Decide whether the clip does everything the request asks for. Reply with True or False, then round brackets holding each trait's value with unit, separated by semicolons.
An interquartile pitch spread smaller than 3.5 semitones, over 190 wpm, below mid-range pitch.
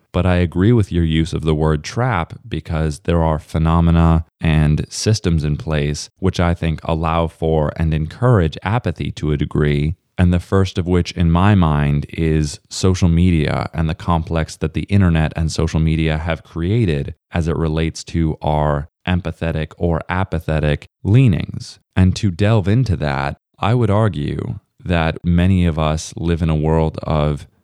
False (2.7 semitones; 165 wpm; 80 Hz)